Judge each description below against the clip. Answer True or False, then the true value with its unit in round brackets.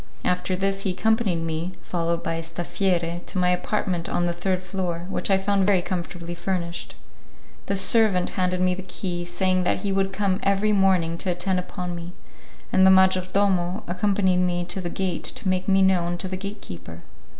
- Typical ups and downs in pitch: False (1.7 semitones)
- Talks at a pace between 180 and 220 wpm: True (195 wpm)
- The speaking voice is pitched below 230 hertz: True (185 Hz)